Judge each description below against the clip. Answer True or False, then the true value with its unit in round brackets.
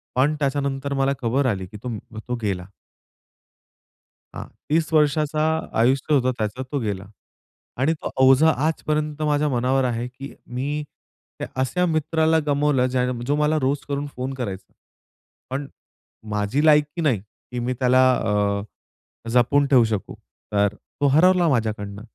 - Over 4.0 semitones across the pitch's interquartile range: False (3.7 semitones)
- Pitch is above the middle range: False (135 Hz)